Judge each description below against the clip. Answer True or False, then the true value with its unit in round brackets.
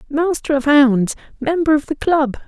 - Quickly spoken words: False (170 wpm)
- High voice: True (290 Hz)